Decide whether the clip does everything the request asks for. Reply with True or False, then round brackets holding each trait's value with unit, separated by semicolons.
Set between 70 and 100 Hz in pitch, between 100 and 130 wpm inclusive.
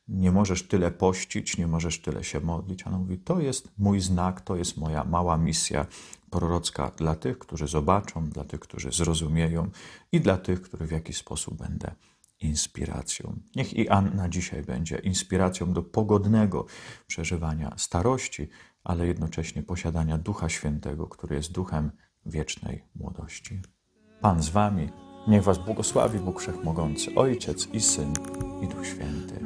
False (90 Hz; 145 wpm)